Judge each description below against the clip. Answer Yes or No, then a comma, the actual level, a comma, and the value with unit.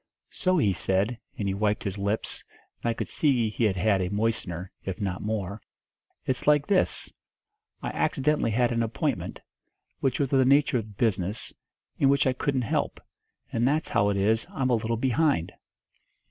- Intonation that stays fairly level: No, average, 4.7 semitones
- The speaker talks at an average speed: Yes, average, 180 wpm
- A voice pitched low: Yes, low, 115 Hz